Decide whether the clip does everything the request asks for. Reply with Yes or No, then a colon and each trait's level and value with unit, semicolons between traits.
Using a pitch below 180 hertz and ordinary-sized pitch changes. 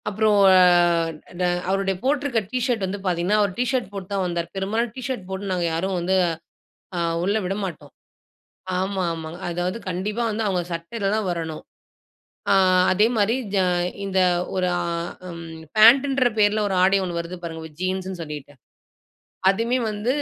No: high, 195 Hz; average, 3.4 semitones